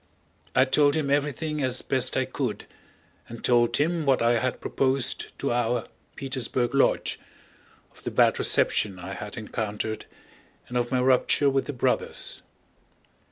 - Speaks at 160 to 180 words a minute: No, average, 150 wpm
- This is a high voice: No, low, 130 Hz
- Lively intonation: No, narrow, 2.6 semitones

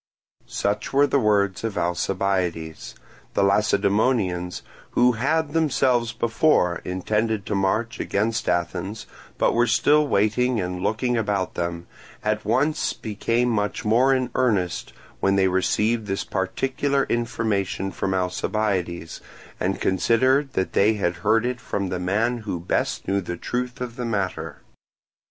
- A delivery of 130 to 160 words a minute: Yes, average, 140 wpm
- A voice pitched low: Yes, low, 105 Hz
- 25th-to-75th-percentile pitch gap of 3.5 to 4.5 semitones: Yes, average, 4.2 semitones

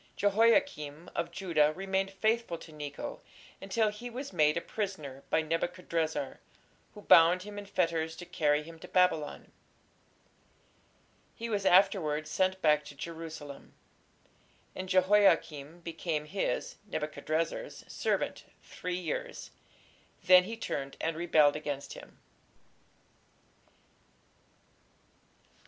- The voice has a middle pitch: Yes, medium, 170 Hz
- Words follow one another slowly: Yes, slow, 110 wpm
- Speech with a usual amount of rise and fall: Yes, average, 4.1 semitones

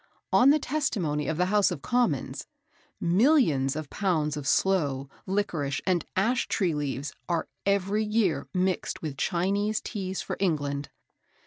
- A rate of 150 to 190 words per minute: No, average, 140 wpm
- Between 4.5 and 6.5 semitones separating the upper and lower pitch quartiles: Yes, wide, 5.5 semitones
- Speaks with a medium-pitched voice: Yes, medium, 180 Hz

